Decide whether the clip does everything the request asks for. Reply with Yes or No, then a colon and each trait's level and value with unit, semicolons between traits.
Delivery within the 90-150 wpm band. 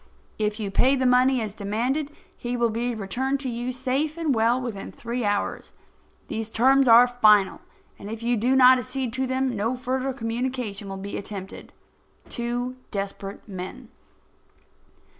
No: average, 160 wpm